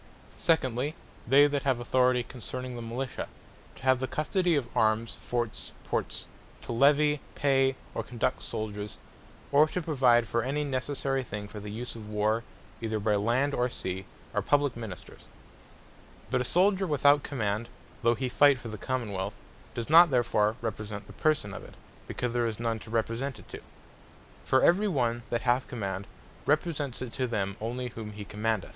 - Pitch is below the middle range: Yes, low, 120 Hz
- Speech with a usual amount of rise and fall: Yes, average, 3.9 semitones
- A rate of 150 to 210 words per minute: Yes, average, 175 wpm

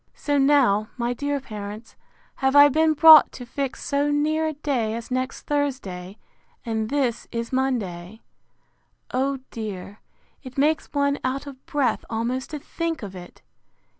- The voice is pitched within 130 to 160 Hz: No, very high, 260 Hz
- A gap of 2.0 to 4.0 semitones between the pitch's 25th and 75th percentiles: No, average, 4.4 semitones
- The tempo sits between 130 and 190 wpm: Yes, average, 150 wpm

